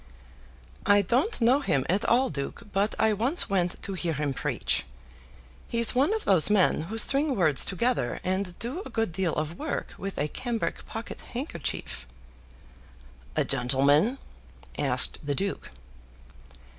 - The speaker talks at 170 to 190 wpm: No, average, 145 wpm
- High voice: Yes, high, 200 Hz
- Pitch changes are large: Yes, wide, 6.7 semitones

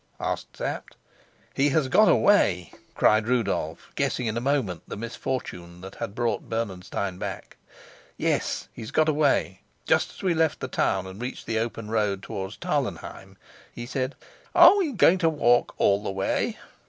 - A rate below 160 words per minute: No, average, 165 wpm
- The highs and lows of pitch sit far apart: Yes, wide, 6.4 semitones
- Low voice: Yes, low, 115 Hz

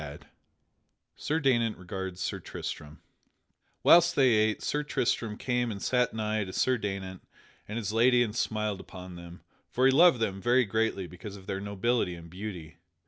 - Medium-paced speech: Yes, average, 170 wpm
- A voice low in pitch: Yes, low, 105 Hz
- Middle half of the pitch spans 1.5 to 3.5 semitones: No, average, 4.5 semitones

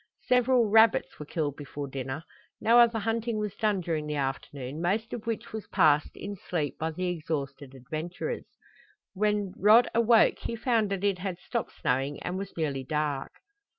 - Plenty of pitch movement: Yes, wide, 6.9 semitones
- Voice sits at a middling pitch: Yes, medium, 180 Hz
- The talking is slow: No, average, 170 wpm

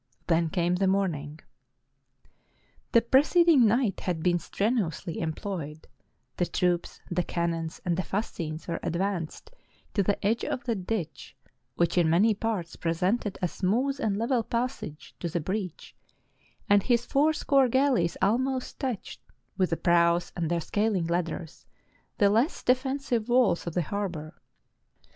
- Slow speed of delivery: No, average, 145 wpm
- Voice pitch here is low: No, high, 190 Hz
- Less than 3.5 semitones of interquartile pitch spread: No, wide, 5.5 semitones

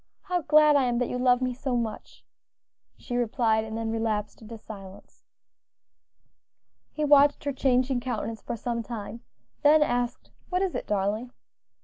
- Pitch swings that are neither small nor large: Yes, average, 3.8 semitones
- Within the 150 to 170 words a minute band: Yes, average, 155 wpm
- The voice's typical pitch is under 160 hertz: No, high, 245 Hz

